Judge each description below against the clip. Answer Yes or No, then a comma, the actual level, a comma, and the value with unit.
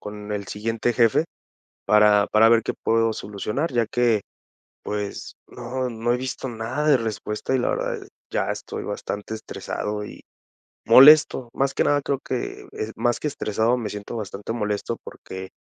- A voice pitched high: No, low, 115 Hz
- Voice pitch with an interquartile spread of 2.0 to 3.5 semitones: Yes, average, 2.9 semitones